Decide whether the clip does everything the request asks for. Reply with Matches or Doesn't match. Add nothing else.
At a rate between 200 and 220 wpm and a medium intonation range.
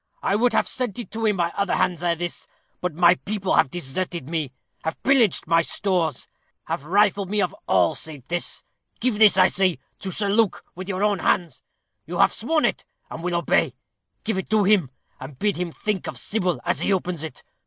Matches